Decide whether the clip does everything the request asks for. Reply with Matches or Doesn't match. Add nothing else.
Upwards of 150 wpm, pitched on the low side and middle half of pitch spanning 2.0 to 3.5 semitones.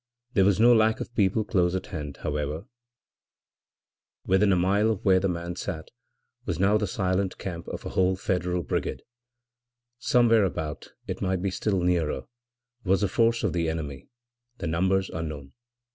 Matches